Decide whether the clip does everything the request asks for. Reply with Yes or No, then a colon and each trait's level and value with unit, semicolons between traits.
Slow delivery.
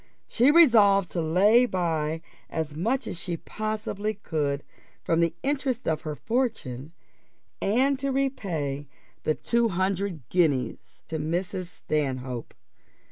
Yes: slow, 125 wpm